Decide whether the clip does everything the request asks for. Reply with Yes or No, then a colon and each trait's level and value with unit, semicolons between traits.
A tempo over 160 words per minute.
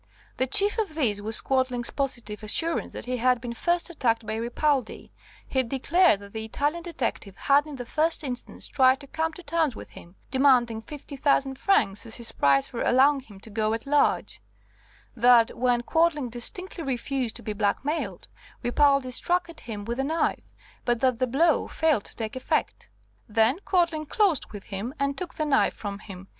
Yes: average, 185 wpm